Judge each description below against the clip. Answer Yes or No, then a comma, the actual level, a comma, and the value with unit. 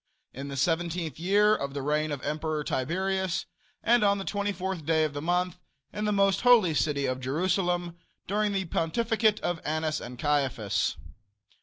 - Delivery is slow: No, average, 165 wpm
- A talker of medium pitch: Yes, medium, 170 Hz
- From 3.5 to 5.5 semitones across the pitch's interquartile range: Yes, average, 4.6 semitones